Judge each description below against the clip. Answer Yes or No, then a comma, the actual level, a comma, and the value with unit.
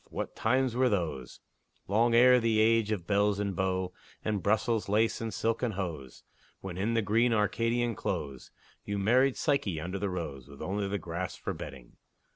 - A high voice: No, low, 105 Hz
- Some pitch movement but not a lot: Yes, average, 3.8 semitones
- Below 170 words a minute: No, average, 175 wpm